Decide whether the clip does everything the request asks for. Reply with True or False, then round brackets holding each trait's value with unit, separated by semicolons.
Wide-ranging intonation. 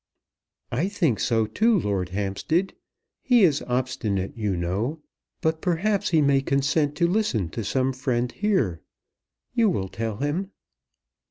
True (8.1 semitones)